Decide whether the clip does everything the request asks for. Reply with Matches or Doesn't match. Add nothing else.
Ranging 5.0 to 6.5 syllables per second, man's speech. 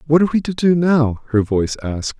Matches